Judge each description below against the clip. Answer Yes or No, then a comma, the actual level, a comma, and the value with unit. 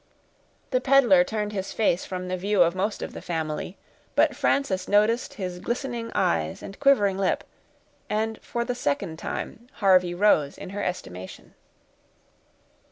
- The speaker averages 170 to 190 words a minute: No, average, 150 wpm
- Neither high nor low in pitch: No, high, 195 Hz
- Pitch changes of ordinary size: Yes, average, 3.9 semitones